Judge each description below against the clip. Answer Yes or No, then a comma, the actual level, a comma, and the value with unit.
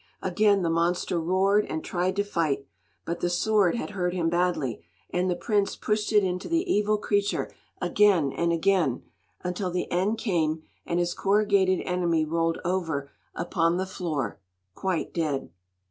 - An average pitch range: Yes, average, 3.0 semitones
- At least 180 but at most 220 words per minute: No, average, 160 wpm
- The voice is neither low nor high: Yes, medium, 180 Hz